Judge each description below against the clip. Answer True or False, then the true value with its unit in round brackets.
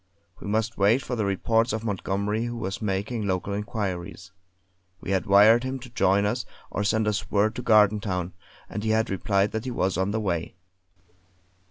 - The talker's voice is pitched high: False (105 Hz)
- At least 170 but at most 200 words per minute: True (185 wpm)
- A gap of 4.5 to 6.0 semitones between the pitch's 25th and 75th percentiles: False (2.4 semitones)